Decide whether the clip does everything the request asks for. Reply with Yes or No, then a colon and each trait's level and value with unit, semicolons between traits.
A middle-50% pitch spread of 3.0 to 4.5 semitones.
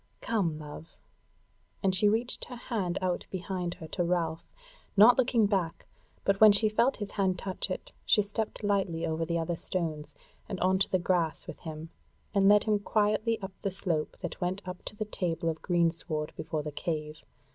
Yes: average, 3.8 semitones